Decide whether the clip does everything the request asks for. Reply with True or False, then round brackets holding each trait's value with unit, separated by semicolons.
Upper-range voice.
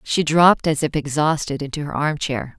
False (150 Hz)